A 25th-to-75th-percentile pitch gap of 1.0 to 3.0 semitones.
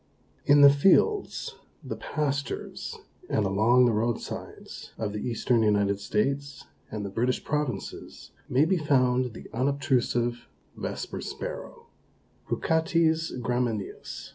No: average, 4.2 semitones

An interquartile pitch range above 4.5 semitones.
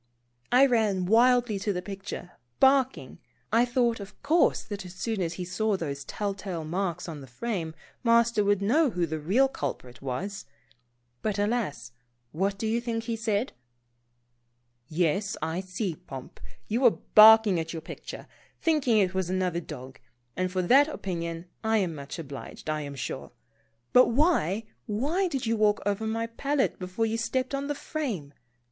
Yes: average, 5.1 semitones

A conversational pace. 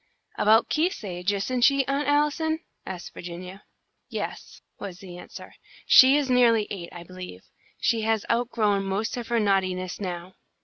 Yes: average, 150 wpm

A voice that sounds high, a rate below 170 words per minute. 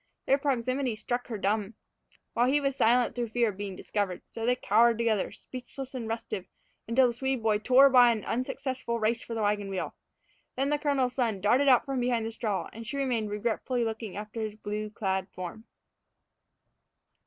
No: high, 230 Hz; average, 190 wpm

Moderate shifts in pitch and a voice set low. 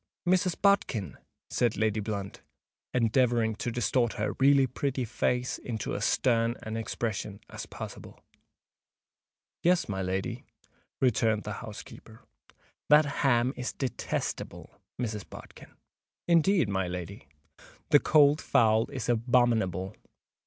Yes: average, 3.7 semitones; low, 115 Hz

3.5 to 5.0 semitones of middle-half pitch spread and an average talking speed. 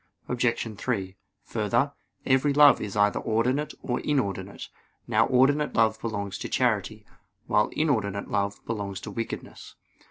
No: average, 4.3 semitones; slow, 130 wpm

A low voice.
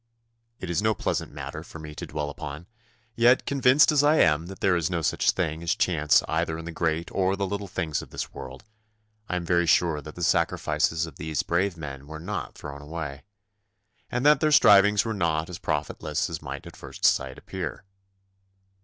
Yes: very low, 85 Hz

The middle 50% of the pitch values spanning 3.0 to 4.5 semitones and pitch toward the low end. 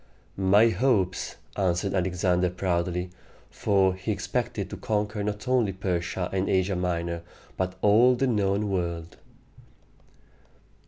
No: narrow, 2.6 semitones; very low, 95 Hz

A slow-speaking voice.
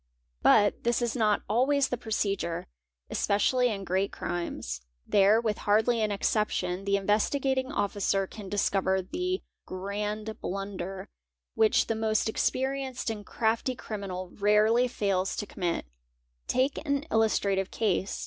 Yes: slow, 130 wpm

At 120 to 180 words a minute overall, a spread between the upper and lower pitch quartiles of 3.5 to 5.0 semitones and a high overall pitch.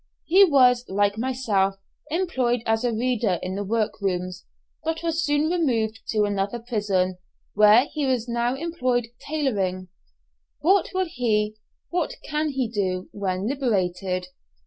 No: average, 140 wpm; wide, 5.4 semitones; high, 230 Hz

